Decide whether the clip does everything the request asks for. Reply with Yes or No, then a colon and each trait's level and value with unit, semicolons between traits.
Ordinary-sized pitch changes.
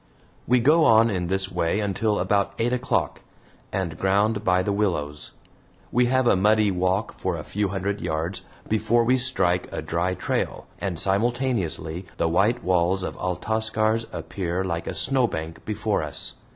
Yes: average, 3.7 semitones